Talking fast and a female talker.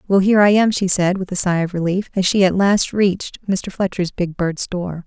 Yes: fast, 250 wpm; female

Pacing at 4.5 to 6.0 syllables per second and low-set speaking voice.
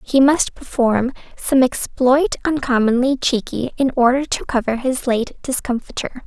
No: 4.6 syllables/s; very high, 255 Hz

